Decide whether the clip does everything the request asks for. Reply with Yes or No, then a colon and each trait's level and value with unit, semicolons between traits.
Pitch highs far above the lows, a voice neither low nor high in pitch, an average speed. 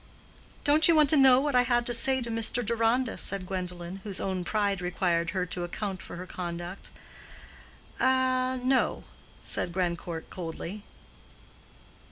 No: wide, 6.1 semitones; high, 205 Hz; average, 145 wpm